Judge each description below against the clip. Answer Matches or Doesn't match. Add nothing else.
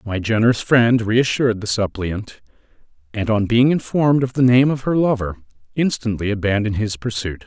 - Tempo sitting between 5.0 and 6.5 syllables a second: Matches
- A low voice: Matches